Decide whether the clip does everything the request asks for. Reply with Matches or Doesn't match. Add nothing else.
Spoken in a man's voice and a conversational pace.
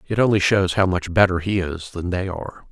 Doesn't match